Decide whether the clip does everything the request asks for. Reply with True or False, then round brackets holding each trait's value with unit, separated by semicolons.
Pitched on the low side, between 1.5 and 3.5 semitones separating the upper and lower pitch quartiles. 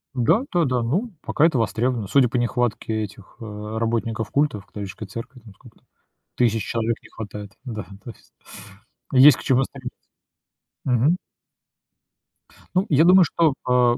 False (115 Hz; 3.9 semitones)